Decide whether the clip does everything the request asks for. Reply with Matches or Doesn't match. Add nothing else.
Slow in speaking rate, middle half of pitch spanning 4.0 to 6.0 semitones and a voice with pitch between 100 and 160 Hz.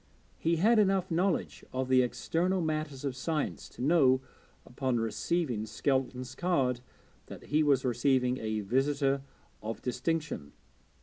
Matches